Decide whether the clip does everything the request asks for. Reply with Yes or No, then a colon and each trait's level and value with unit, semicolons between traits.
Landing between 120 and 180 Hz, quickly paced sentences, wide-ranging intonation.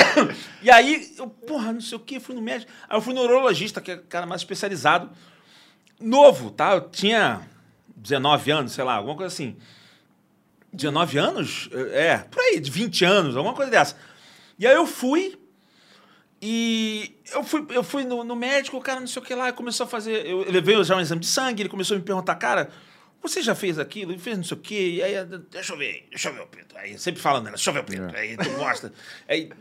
No: high, 210 Hz; fast, 225 wpm; wide, 5.8 semitones